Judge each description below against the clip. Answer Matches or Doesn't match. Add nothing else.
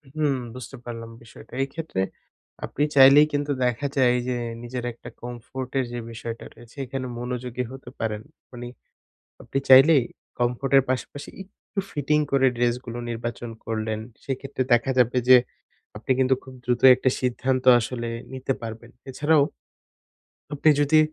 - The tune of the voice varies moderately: Doesn't match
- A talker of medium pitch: Doesn't match